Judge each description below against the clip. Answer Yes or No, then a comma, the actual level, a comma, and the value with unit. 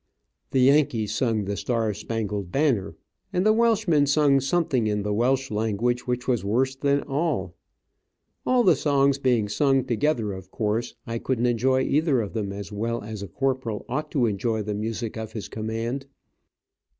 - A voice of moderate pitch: No, low, 120 Hz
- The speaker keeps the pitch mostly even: No, average, 4.3 semitones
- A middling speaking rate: Yes, average, 170 wpm